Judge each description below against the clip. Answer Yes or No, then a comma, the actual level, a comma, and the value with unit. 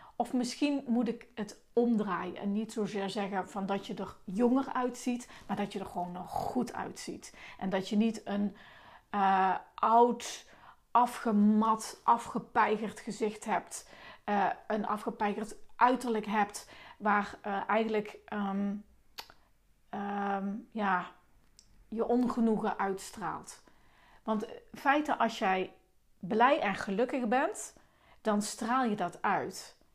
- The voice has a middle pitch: No, high, 215 Hz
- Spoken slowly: Yes, slow, 125 wpm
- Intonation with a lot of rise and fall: No, average, 2.9 semitones